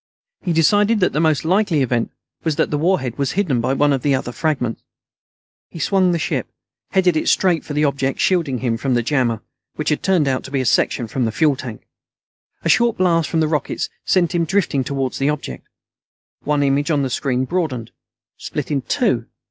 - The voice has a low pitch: No, medium, 145 Hz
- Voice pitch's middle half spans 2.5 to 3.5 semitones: No, average, 4.3 semitones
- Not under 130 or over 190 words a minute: No, fast, 205 wpm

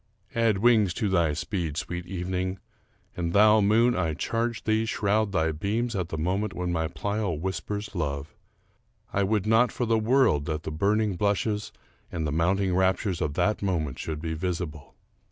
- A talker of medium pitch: No, very low, 95 Hz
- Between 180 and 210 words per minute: No, average, 170 wpm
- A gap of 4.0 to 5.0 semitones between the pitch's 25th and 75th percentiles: Yes, average, 4.4 semitones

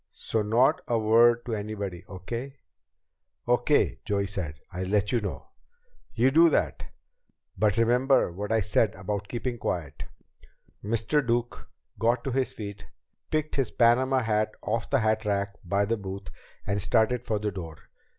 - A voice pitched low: Yes, low, 110 Hz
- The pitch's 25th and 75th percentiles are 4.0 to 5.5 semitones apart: No, average, 3.2 semitones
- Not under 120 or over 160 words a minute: Yes, average, 150 wpm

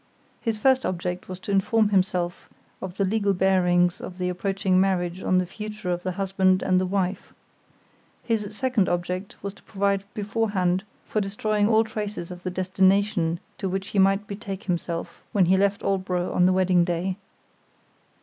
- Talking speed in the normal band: Yes, average, 170 wpm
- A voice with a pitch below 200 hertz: Yes, high, 190 Hz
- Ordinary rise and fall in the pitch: No, narrow, 1.9 semitones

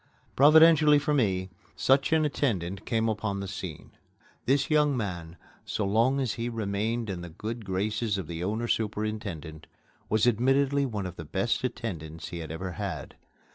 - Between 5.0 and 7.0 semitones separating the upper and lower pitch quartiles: Yes, wide, 5.4 semitones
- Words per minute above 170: No, average, 165 wpm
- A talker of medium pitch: No, low, 110 Hz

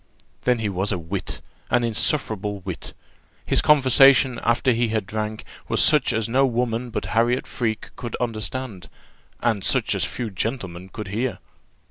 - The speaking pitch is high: No, low, 115 Hz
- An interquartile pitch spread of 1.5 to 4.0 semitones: Yes, average, 3.2 semitones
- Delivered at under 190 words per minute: Yes, average, 155 wpm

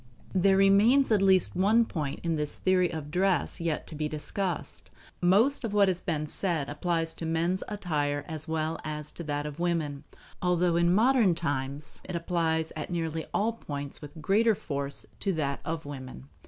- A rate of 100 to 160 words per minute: No, average, 180 wpm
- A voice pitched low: No, medium, 165 Hz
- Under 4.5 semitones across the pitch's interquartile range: Yes, average, 4.0 semitones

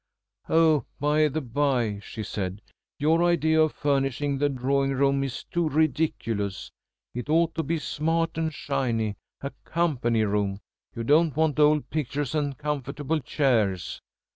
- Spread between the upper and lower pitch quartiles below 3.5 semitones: No, average, 4.2 semitones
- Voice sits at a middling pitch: Yes, medium, 145 Hz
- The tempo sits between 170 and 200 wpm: No, average, 140 wpm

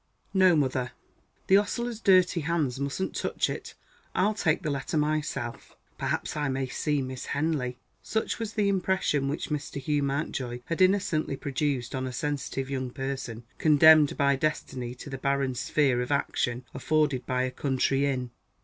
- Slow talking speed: No, average, 160 wpm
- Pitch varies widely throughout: No, average, 3.3 semitones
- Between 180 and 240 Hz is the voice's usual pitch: No, medium, 140 Hz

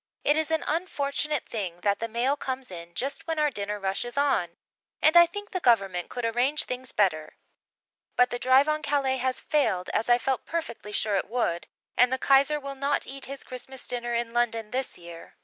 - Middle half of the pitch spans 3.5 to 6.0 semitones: Yes, average, 4.7 semitones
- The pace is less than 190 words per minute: No, fast, 205 wpm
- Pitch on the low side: No, very high, 255 Hz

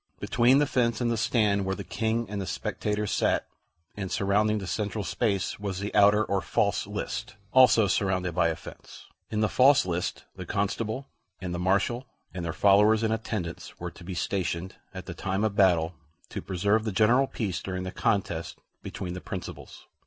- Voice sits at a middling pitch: No, low, 100 Hz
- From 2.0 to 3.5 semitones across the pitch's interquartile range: Yes, average, 3.1 semitones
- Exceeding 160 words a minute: Yes, average, 190 wpm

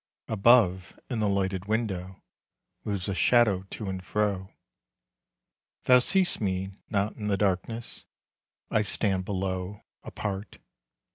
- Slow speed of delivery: Yes, slow, 120 wpm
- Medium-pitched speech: No, low, 100 Hz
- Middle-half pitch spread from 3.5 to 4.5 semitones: No, narrow, 2.4 semitones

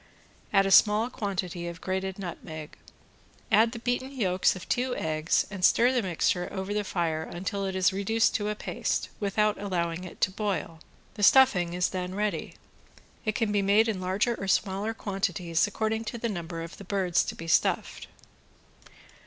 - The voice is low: No, high, 195 Hz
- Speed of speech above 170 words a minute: Yes, average, 180 wpm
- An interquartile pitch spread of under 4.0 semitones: Yes, average, 3.0 semitones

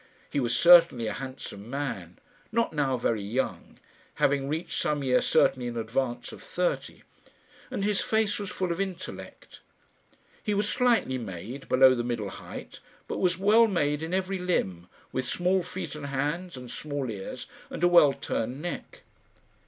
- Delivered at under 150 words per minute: No, average, 165 wpm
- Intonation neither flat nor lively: No, wide, 6.7 semitones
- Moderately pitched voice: Yes, medium, 145 Hz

